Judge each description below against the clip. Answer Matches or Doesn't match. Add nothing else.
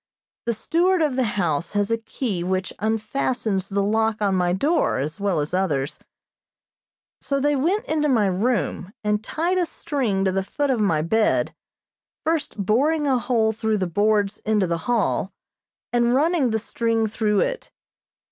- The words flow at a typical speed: Matches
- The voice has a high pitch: Matches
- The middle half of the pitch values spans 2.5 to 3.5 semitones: Doesn't match